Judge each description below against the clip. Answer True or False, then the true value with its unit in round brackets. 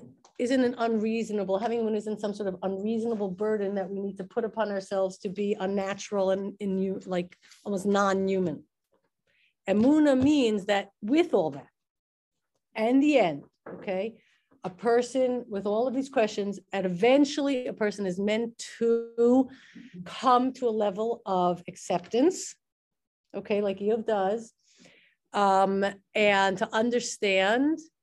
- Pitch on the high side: True (210 Hz)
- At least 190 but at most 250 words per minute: False (140 wpm)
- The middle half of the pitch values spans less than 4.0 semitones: True (3.3 semitones)